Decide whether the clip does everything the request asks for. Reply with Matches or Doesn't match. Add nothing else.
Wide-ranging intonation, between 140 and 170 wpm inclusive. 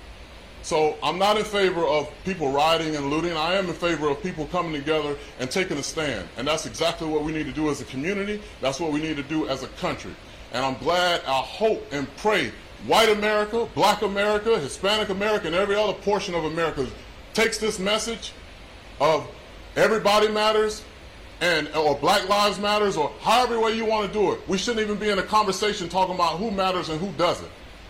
Doesn't match